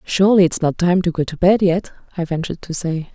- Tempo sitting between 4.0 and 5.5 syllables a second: No, 6.1 syllables/s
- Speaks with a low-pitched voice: No, medium, 175 Hz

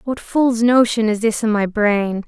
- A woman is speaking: Yes, female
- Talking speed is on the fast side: Yes, fast, 210 wpm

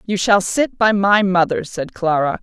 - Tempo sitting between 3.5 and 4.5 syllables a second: Yes, 4.4 syllables/s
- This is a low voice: No, high, 190 Hz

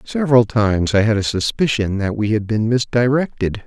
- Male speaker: Yes, male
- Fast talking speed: No, average, 180 wpm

